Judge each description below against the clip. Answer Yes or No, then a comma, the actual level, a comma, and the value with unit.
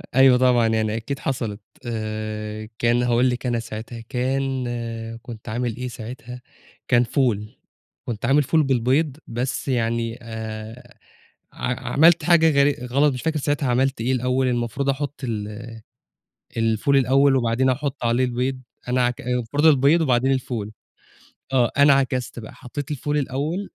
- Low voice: Yes, low, 125 Hz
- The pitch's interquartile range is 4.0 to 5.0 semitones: No, average, 2.7 semitones